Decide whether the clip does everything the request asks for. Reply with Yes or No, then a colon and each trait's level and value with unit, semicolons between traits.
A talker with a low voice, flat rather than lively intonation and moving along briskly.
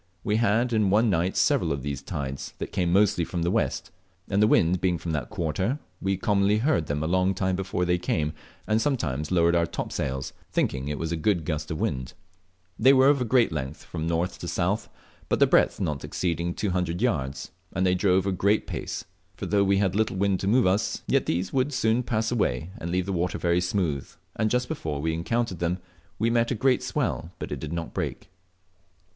No: very low, 90 Hz; average, 4.5 semitones; fast, 210 wpm